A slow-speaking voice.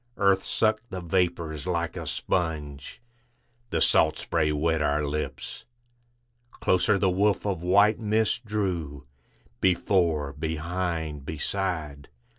Yes: slow, 110 wpm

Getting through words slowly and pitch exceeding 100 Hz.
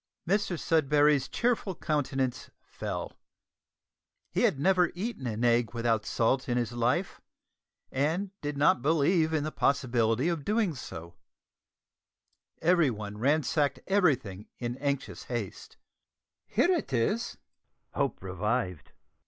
Yes: slow, 110 wpm; medium, 140 Hz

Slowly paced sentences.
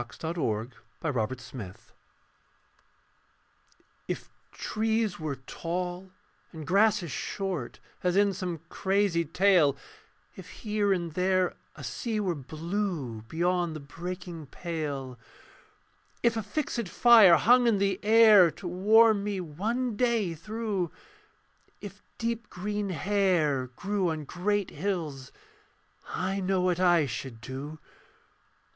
Yes: slow, 120 wpm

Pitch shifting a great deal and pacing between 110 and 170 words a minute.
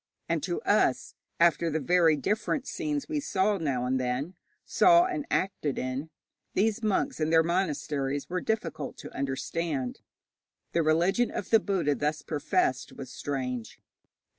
Yes: wide, 6.5 semitones; average, 145 wpm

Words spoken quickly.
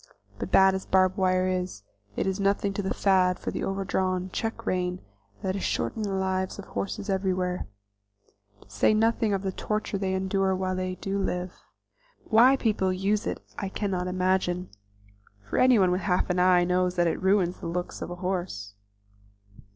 No: average, 180 wpm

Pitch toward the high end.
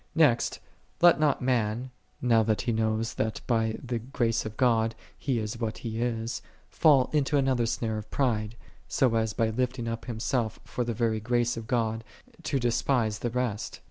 No: low, 115 Hz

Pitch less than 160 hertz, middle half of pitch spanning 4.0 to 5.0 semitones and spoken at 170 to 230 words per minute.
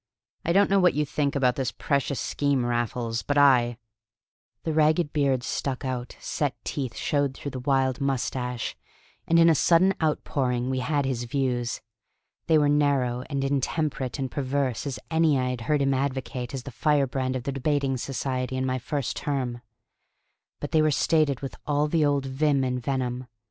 No: low, 135 Hz; narrow, 2.4 semitones; average, 180 wpm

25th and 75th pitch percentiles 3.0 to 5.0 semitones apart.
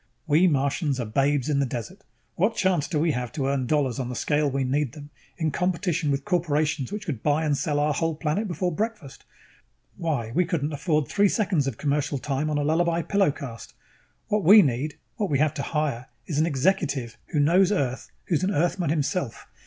Yes: average, 3.8 semitones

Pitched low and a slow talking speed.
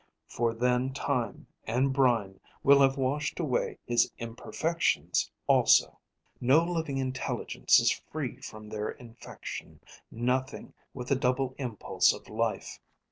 Yes: low, 130 Hz; slow, 125 wpm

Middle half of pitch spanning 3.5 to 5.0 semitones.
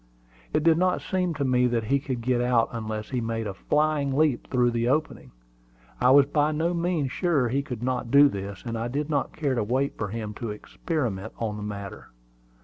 Yes: average, 4.4 semitones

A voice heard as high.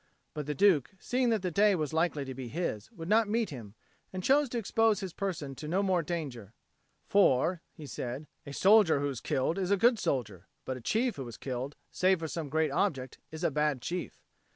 No: medium, 160 Hz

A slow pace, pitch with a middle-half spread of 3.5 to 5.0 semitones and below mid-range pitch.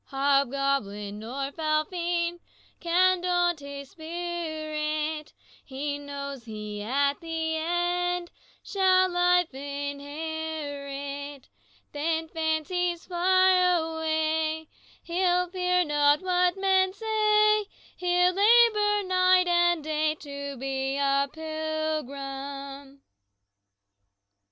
No: slow, 90 wpm; average, 4.0 semitones; very high, 315 Hz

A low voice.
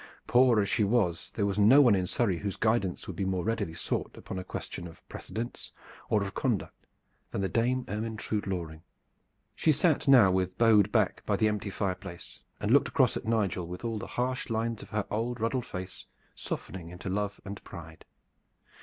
Yes: low, 105 Hz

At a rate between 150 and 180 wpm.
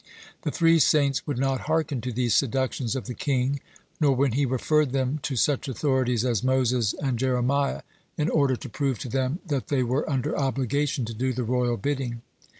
No: average, 190 wpm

